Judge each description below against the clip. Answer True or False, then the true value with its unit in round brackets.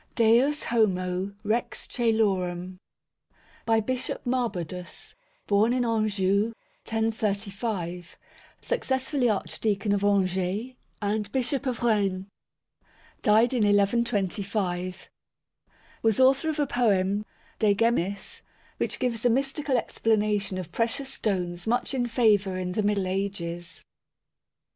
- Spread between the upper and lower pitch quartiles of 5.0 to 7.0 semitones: False (3.8 semitones)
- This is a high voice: True (210 Hz)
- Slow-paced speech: True (105 wpm)